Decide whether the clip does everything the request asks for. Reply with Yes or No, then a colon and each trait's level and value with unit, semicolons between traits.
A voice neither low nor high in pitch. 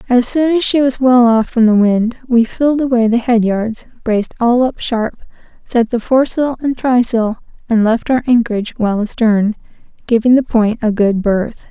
No: high, 235 Hz